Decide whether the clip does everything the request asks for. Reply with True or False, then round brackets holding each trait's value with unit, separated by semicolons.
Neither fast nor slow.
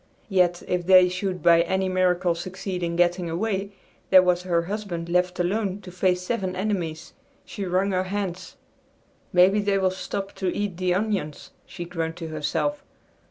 True (165 wpm)